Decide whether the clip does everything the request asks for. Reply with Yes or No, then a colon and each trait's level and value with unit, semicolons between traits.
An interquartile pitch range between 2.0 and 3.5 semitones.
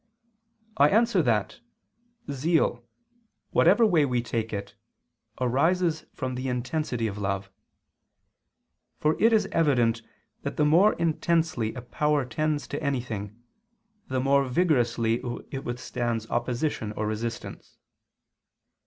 No: average, 5.1 semitones